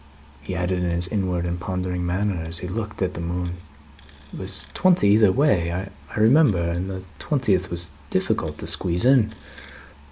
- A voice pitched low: Yes, very low, 90 Hz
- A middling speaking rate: Yes, average, 170 wpm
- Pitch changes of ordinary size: Yes, average, 3.2 semitones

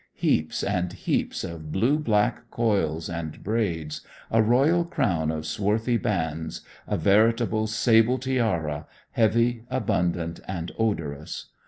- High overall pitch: No, low, 105 Hz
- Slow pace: Yes, slow, 120 wpm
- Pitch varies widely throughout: Yes, wide, 6.0 semitones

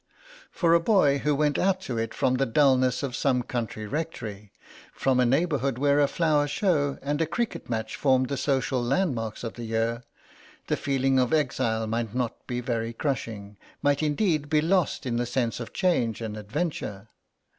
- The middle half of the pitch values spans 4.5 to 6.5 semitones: No, average, 4.1 semitones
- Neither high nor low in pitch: No, low, 130 Hz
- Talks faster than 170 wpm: Yes, average, 180 wpm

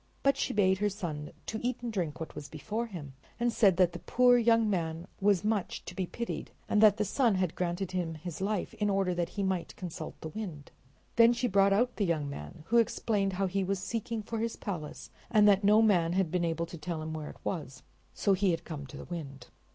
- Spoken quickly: Yes, fast, 235 wpm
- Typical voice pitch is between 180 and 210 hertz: Yes, high, 190 Hz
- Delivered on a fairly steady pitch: No, average, 4.2 semitones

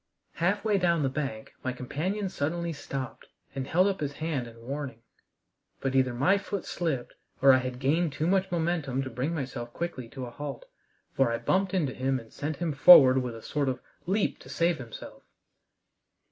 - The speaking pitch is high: No, medium, 140 Hz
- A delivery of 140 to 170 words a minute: No, average, 190 wpm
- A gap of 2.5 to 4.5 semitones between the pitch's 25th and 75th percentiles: No, average, 5.0 semitones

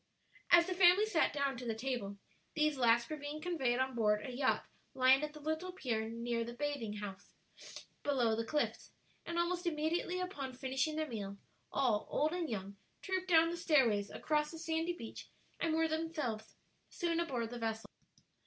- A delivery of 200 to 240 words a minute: No, average, 180 wpm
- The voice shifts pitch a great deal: Yes, wide, 5.8 semitones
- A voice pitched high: Yes, very high, 285 Hz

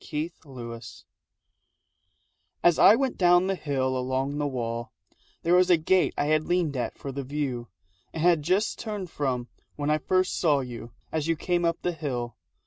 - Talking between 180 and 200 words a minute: Yes, average, 185 wpm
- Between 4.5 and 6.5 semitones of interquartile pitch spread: Yes, average, 5.1 semitones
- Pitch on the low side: No, medium, 150 Hz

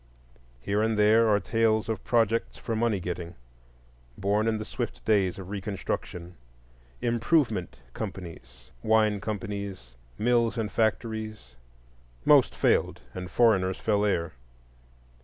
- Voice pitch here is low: Yes, low, 105 Hz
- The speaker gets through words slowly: Yes, slow, 120 wpm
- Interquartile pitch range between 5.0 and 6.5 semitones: No, average, 3.8 semitones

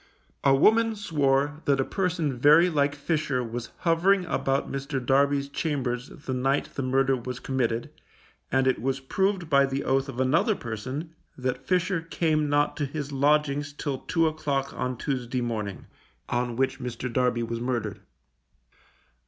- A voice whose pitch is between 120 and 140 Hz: Yes, low, 135 Hz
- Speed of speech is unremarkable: Yes, average, 155 wpm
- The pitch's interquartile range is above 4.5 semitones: No, average, 3.0 semitones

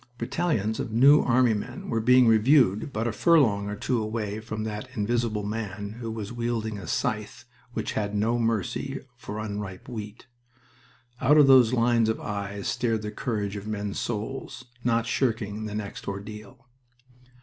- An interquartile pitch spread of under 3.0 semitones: Yes, narrow, 2.5 semitones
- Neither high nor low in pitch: No, low, 110 Hz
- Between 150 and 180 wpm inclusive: Yes, average, 160 wpm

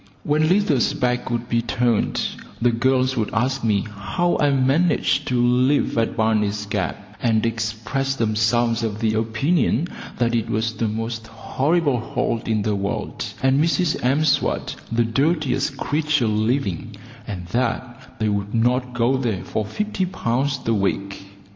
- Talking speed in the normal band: Yes, average, 150 wpm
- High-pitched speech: No, low, 120 Hz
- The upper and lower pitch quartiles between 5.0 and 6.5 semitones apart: No, average, 3.7 semitones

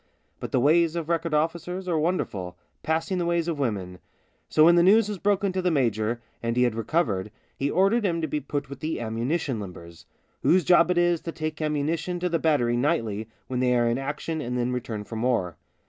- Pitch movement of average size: No, wide, 6.2 semitones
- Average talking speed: No, fast, 220 wpm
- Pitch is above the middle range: No, medium, 150 Hz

